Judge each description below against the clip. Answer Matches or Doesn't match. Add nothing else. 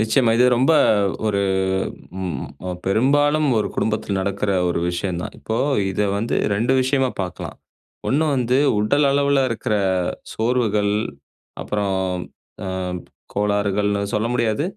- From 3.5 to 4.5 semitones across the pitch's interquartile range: Matches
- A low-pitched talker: Matches